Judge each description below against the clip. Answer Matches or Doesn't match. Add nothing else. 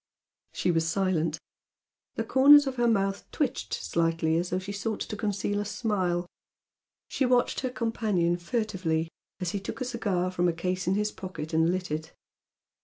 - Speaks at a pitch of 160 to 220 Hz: Matches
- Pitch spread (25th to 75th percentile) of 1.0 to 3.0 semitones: Doesn't match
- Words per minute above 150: Matches